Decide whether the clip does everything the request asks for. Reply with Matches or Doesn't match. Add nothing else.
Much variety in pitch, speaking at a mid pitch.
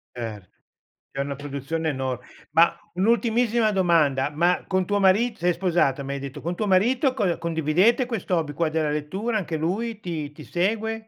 Matches